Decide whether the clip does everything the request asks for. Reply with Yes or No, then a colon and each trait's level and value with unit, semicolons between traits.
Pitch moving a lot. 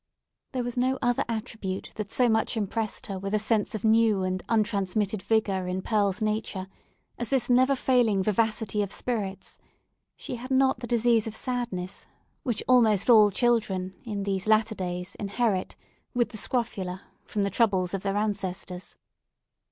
No: average, 3.3 semitones